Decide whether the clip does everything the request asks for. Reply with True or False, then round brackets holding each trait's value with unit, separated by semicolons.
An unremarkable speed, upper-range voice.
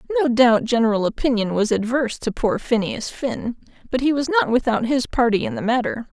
True (195 wpm; 235 Hz)